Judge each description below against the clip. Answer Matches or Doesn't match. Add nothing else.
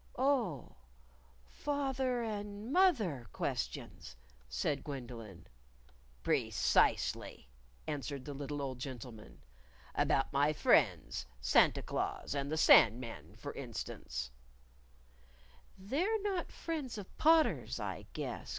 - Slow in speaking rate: Matches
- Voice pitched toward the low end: Doesn't match